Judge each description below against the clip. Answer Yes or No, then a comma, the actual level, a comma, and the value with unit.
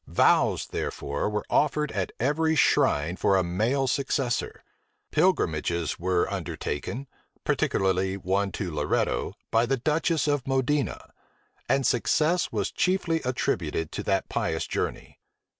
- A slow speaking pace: Yes, slow, 125 wpm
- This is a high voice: No, low, 120 Hz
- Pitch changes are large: Yes, wide, 8.1 semitones